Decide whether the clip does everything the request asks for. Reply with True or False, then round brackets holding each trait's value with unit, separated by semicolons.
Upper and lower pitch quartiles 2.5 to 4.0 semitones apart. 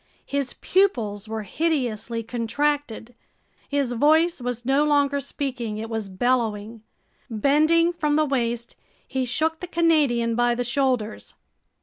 False (4.4 semitones)